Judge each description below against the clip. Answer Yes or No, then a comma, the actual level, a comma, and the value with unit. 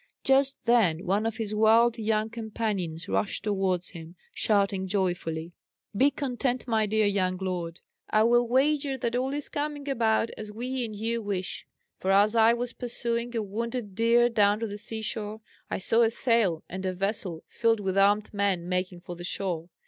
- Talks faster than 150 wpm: Yes, average, 180 wpm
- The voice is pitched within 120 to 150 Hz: No, high, 215 Hz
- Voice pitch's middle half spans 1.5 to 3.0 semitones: No, average, 3.6 semitones